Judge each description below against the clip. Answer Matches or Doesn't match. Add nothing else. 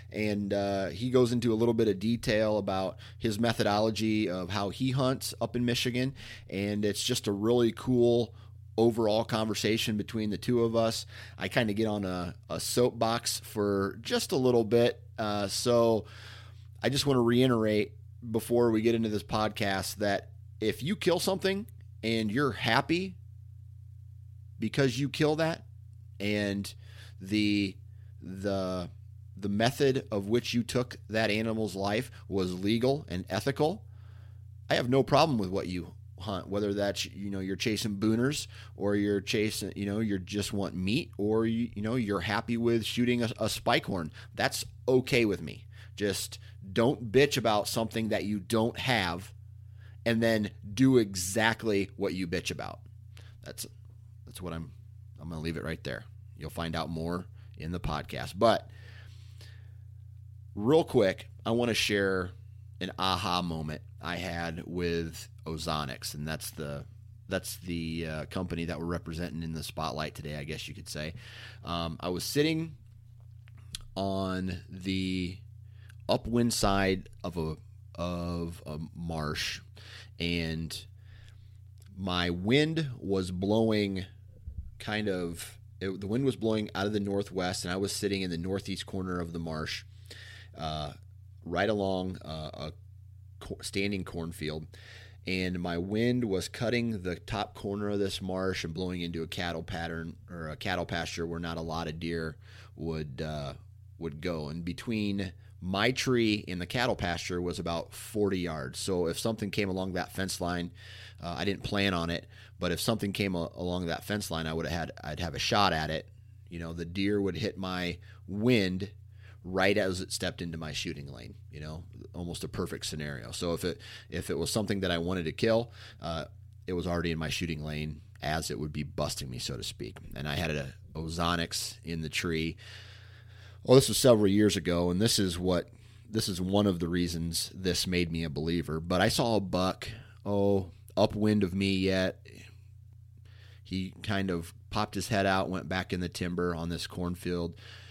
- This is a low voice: Matches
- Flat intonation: Doesn't match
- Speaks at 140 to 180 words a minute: Matches